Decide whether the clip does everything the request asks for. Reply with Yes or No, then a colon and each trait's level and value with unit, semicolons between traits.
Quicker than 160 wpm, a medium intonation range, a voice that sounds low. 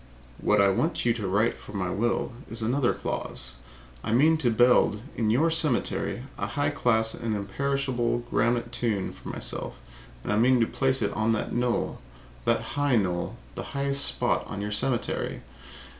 Yes: average, 170 wpm; average, 3.7 semitones; low, 120 Hz